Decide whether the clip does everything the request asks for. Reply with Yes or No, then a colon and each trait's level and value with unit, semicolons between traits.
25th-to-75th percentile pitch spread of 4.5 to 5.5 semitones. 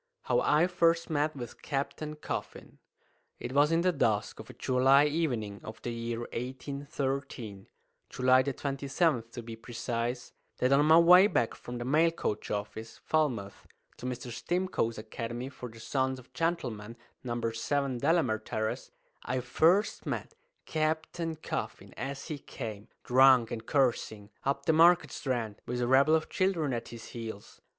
Yes: average, 4.8 semitones